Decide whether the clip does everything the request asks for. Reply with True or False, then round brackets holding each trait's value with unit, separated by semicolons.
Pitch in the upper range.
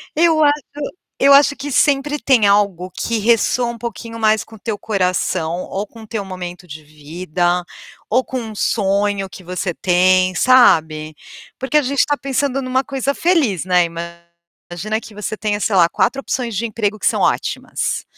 True (210 Hz)